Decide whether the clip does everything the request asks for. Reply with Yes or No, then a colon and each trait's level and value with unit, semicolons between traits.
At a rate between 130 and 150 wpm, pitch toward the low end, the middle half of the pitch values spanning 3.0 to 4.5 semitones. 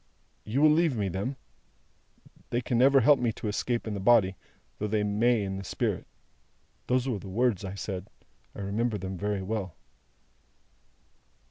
No: average, 165 wpm; low, 105 Hz; average, 3.8 semitones